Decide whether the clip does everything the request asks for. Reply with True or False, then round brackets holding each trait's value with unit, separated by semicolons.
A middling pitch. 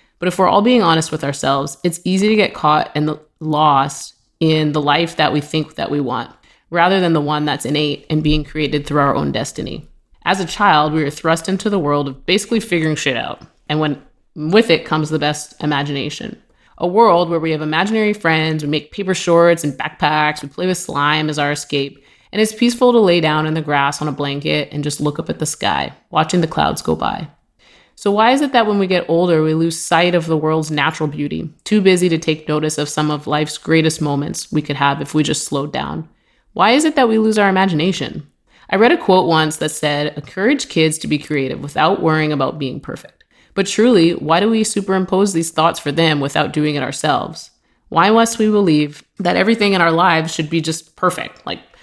True (155 Hz)